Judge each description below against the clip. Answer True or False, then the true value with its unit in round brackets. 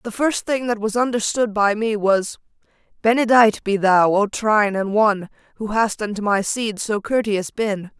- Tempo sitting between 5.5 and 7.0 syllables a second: False (4.7 syllables/s)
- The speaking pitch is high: True (215 Hz)